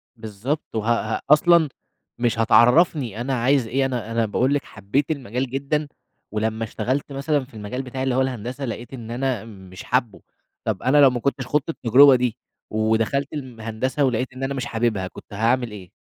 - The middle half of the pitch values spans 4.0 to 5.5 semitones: No, average, 3.3 semitones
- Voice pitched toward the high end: No, low, 125 Hz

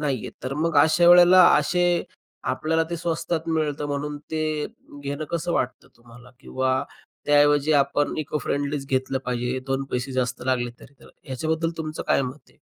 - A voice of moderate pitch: Yes, medium, 145 Hz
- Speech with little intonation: No, average, 3.4 semitones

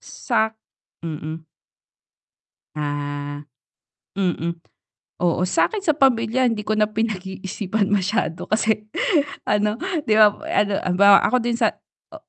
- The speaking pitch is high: Yes, high, 205 Hz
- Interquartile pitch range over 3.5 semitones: Yes, average, 4.2 semitones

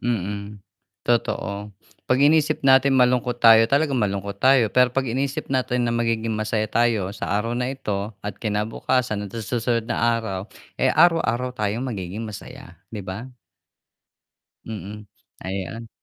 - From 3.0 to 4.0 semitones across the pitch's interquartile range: Yes, average, 3.5 semitones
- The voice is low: Yes, low, 115 Hz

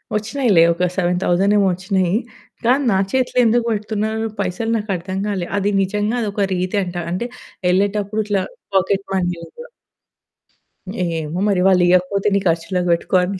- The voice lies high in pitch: Yes, high, 195 Hz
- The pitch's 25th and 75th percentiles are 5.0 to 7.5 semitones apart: No, average, 2.7 semitones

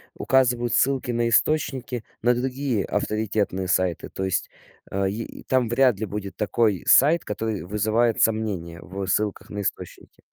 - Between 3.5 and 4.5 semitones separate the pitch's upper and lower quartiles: Yes, average, 3.8 semitones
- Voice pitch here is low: Yes, low, 110 Hz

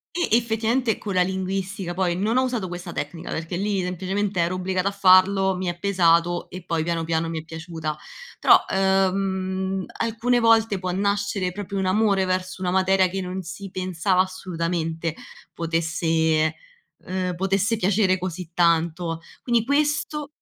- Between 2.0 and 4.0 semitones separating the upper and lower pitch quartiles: Yes, narrow, 2.6 semitones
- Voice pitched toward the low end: No, medium, 185 Hz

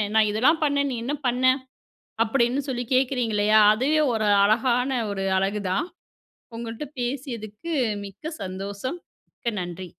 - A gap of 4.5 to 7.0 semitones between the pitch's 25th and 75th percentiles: No, average, 4.0 semitones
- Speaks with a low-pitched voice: No, high, 235 Hz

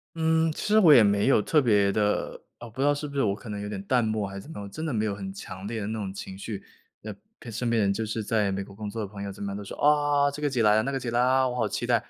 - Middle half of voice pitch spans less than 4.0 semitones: No, average, 5.0 semitones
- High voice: No, low, 110 Hz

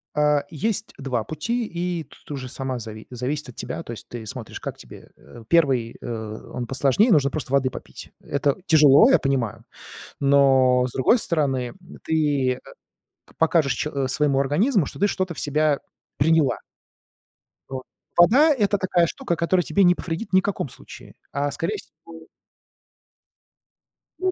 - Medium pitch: Yes, medium, 145 Hz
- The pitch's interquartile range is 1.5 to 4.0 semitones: No, average, 4.7 semitones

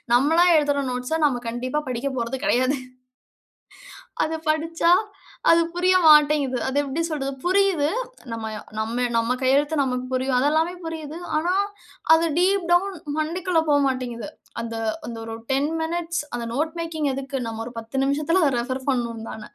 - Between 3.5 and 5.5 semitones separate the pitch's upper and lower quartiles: Yes, average, 4.3 semitones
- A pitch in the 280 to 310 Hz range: Yes, very high, 285 Hz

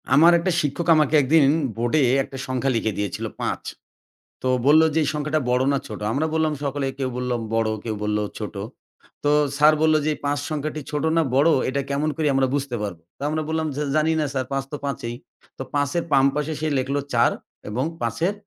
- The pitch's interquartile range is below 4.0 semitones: Yes, average, 3.3 semitones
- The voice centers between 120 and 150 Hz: Yes, medium, 140 Hz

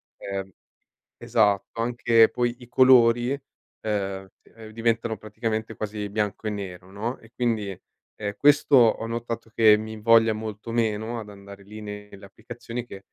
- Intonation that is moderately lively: No, narrow, 2.2 semitones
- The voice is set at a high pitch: No, low, 110 Hz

